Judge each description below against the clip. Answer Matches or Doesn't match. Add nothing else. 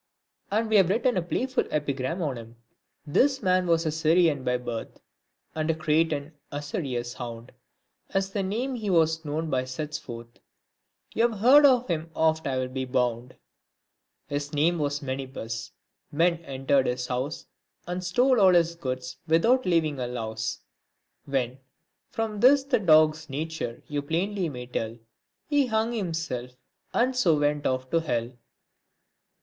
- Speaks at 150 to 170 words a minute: Matches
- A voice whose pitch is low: Doesn't match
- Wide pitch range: Matches